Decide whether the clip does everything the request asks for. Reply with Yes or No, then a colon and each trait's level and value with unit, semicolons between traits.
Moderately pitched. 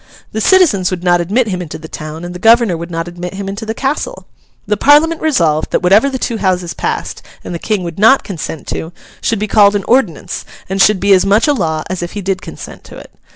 No: high, 195 Hz